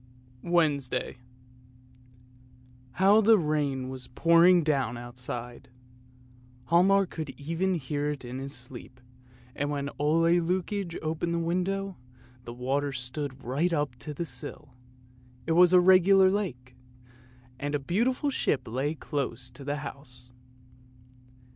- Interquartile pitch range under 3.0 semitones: No, average, 5.1 semitones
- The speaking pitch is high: No, medium, 150 Hz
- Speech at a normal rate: No, slow, 130 wpm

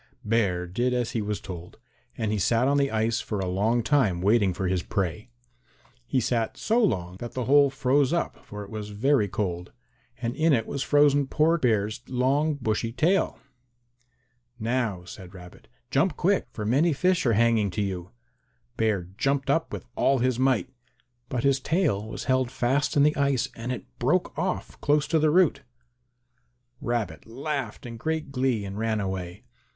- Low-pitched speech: Yes, low, 120 Hz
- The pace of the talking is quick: No, average, 175 wpm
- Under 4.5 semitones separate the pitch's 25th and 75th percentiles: No, average, 5.3 semitones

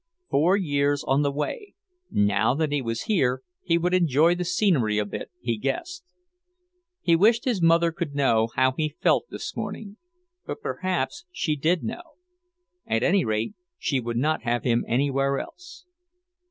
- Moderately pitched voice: Yes, medium, 150 Hz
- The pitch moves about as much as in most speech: No, wide, 5.9 semitones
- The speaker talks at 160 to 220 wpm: Yes, average, 165 wpm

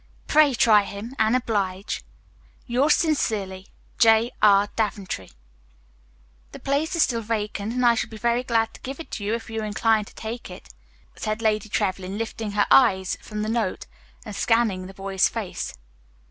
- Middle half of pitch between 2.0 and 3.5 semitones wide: Yes, average, 2.7 semitones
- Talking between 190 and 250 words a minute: No, average, 170 wpm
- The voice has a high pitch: Yes, high, 220 Hz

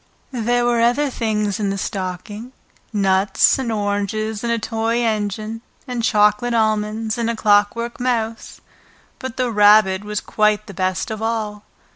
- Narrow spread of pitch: Yes, narrow, 2.1 semitones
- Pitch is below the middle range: No, high, 215 Hz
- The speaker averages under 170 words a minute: Yes, average, 150 wpm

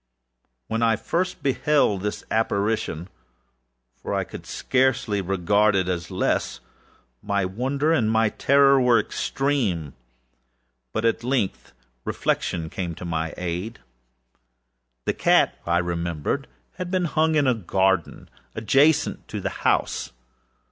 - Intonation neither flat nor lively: No, wide, 6.9 semitones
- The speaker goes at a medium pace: No, slow, 120 wpm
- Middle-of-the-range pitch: No, low, 110 Hz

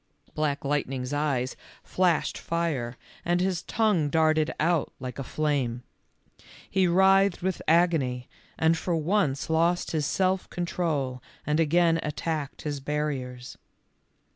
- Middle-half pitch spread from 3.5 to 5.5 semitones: Yes, average, 3.8 semitones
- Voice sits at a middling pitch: Yes, medium, 155 Hz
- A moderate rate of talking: No, slow, 120 wpm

